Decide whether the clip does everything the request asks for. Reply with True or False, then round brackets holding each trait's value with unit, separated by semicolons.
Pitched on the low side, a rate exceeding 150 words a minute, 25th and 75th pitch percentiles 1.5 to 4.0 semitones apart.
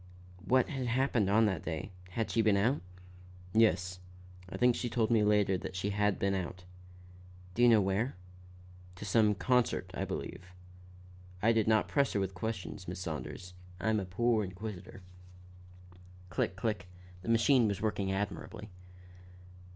True (105 Hz; 160 wpm; 3.4 semitones)